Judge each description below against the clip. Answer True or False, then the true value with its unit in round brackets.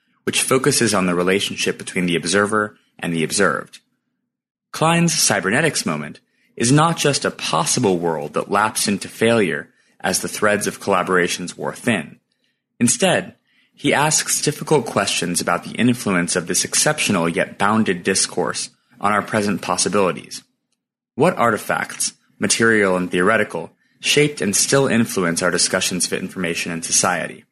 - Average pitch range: False (7.5 semitones)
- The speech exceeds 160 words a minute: False (140 wpm)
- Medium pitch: False (105 Hz)